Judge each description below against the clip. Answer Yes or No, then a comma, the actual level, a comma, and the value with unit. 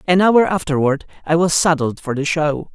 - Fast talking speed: No, average, 195 wpm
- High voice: No, medium, 160 Hz